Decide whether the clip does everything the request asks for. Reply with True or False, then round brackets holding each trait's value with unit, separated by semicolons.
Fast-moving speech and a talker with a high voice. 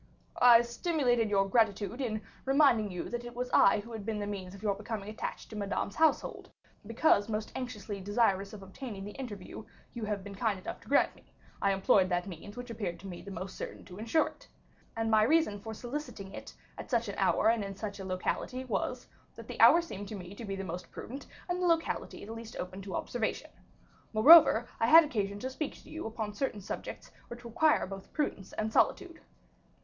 True (210 wpm; 215 Hz)